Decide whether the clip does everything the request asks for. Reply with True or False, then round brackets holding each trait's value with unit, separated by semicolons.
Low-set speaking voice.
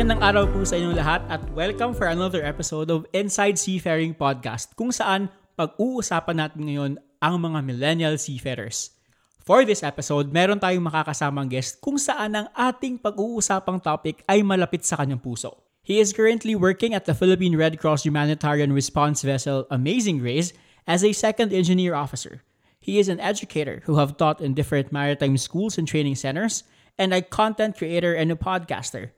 False (165 Hz)